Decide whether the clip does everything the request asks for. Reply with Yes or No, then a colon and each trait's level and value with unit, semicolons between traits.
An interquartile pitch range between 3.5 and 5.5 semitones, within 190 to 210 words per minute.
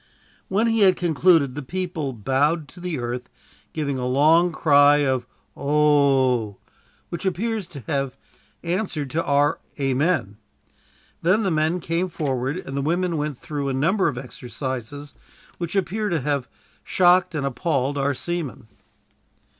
No: average, 4.5 semitones; average, 145 wpm